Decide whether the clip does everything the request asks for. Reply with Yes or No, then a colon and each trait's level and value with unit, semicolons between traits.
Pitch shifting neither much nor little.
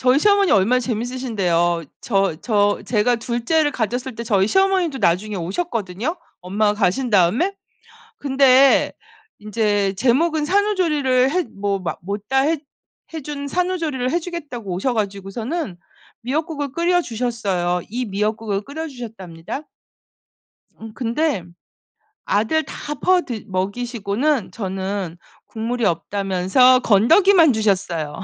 No: wide, 6.5 semitones